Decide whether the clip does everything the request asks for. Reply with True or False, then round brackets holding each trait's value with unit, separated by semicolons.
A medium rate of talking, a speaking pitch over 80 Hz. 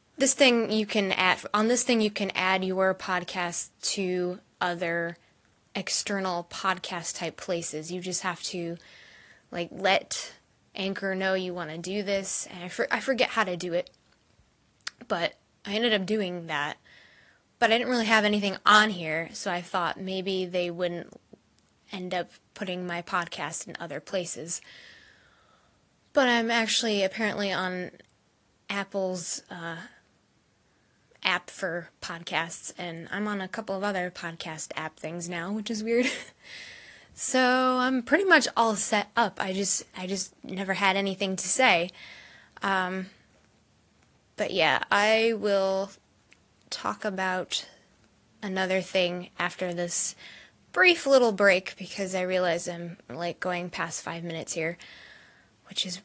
True (145 wpm; 190 Hz)